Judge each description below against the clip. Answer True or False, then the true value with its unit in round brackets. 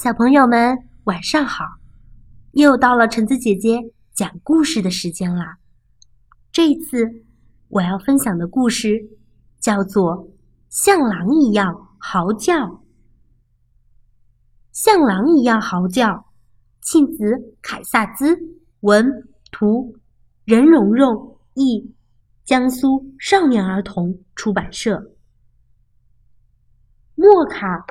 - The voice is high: True (215 Hz)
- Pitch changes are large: True (7.2 semitones)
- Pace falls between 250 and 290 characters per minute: False (150 characters per minute)